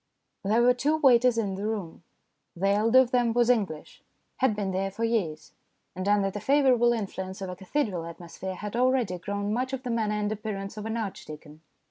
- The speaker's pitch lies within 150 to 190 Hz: No, high, 210 Hz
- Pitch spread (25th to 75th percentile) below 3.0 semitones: No, average, 3.9 semitones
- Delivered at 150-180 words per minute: No, average, 195 wpm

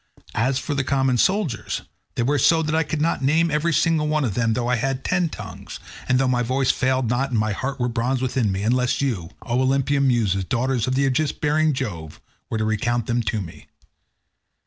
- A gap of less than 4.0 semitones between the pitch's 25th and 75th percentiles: Yes, average, 3.2 semitones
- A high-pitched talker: No, low, 130 Hz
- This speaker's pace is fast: Yes, fast, 215 wpm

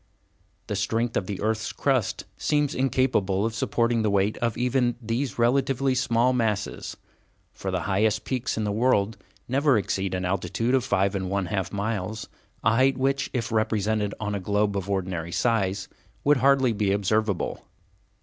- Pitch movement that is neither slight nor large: Yes, average, 4.1 semitones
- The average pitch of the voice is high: No, low, 110 Hz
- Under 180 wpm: Yes, average, 165 wpm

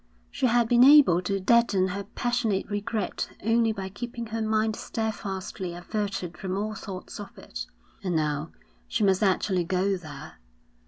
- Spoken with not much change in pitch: No, average, 3.4 semitones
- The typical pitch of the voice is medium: No, high, 200 Hz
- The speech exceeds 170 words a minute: No, average, 155 wpm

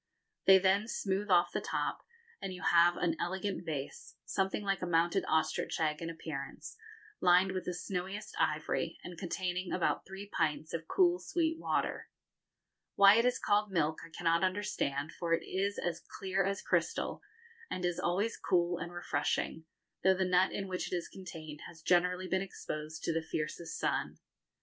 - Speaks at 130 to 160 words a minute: No, average, 175 wpm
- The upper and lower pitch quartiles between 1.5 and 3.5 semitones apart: Yes, narrow, 2.6 semitones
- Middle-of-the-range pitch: Yes, medium, 180 Hz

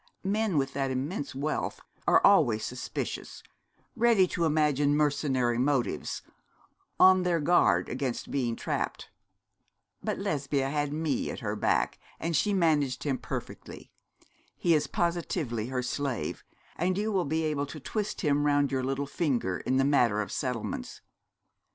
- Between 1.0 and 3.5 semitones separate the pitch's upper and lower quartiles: No, average, 4.0 semitones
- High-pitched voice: No, medium, 145 Hz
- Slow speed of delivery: No, average, 145 wpm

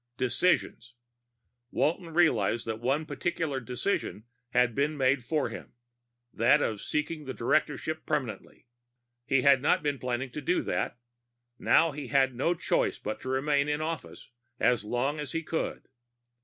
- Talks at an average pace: Yes, average, 150 wpm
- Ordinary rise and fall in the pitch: Yes, average, 3.8 semitones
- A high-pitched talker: No, medium, 140 Hz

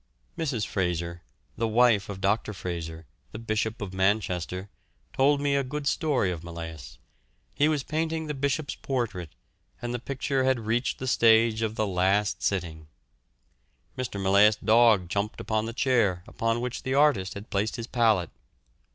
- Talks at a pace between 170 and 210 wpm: No, average, 160 wpm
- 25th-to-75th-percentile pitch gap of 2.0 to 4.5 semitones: No, average, 5.2 semitones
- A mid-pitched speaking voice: No, low, 110 Hz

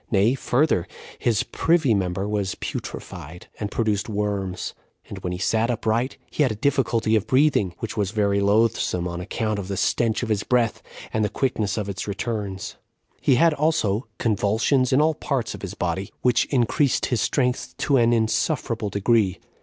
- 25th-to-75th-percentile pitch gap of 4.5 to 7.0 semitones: No, average, 3.6 semitones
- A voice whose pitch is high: No, low, 110 Hz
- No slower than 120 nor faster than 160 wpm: No, average, 175 wpm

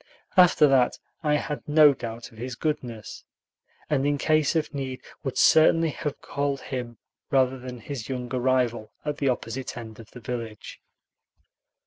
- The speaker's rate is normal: Yes, average, 155 wpm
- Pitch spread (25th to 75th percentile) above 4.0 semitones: No, average, 3.5 semitones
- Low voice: Yes, low, 130 Hz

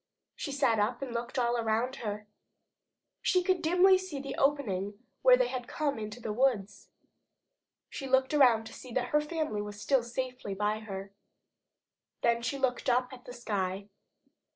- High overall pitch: Yes, high, 245 Hz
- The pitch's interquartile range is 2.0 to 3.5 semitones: No, average, 4.4 semitones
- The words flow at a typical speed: Yes, average, 170 wpm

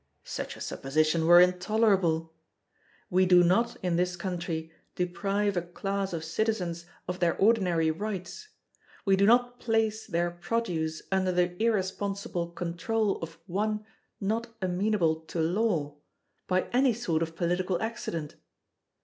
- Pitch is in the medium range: Yes, medium, 180 Hz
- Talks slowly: Yes, slow, 130 wpm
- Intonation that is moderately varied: Yes, average, 3.8 semitones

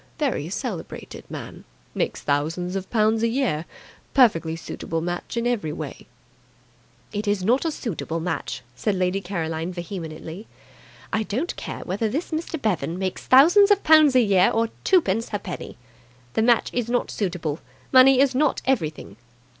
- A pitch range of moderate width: No, wide, 6.6 semitones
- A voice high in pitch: Yes, high, 205 Hz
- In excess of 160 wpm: No, average, 155 wpm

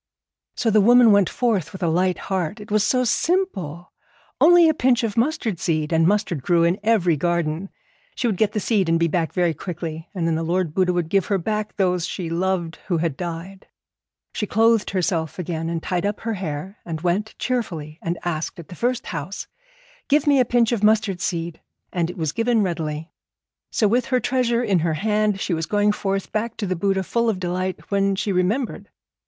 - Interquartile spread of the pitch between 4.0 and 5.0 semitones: Yes, average, 4.3 semitones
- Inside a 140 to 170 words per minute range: No, fast, 205 wpm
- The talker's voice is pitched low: No, high, 190 Hz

